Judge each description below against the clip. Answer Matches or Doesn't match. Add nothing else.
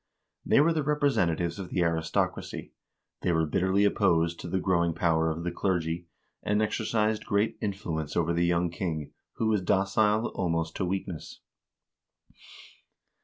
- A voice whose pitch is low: Matches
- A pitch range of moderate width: Matches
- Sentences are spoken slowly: Doesn't match